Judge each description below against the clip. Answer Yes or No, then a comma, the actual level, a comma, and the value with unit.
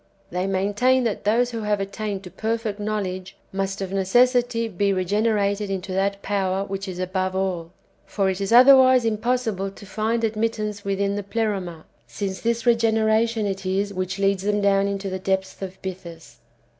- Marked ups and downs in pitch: No, narrow, 2.6 semitones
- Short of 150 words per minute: No, average, 170 wpm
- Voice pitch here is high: Yes, high, 200 Hz